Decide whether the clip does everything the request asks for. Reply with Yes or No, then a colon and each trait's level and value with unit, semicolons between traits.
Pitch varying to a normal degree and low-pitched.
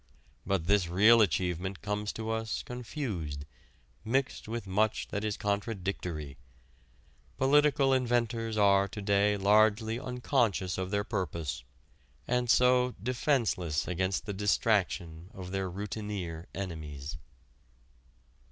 Yes: average, 3.8 semitones; low, 105 Hz